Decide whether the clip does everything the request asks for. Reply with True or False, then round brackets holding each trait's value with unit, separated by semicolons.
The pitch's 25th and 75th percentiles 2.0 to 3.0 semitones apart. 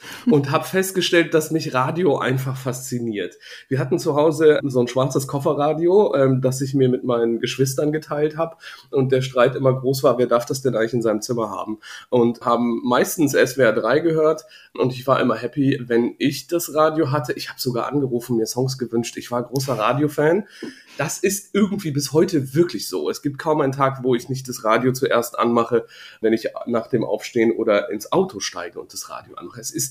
False (4.2 semitones)